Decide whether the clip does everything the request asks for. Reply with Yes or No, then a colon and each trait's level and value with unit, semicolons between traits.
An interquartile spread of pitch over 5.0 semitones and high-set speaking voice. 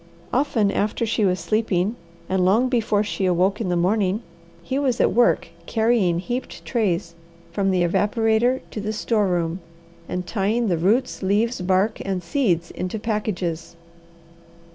No: average, 3.9 semitones; high, 205 Hz